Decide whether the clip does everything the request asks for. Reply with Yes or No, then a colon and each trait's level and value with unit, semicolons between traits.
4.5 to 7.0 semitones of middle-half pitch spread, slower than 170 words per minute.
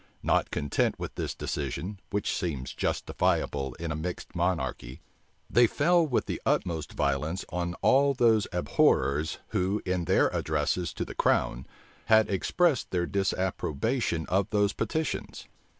Yes: wide, 5.5 semitones; slow, 135 wpm